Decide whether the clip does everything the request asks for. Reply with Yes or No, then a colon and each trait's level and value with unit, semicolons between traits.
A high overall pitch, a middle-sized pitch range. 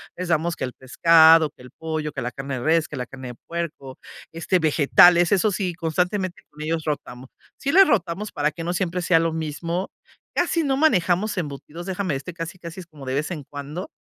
No: medium, 165 Hz; average, 3.3 semitones